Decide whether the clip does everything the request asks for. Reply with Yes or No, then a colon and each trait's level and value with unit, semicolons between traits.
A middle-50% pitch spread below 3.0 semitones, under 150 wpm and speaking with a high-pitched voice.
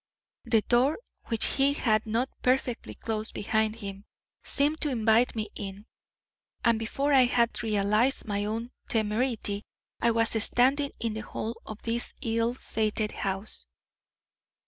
Yes: narrow, 2.4 semitones; average, 140 wpm; high, 225 Hz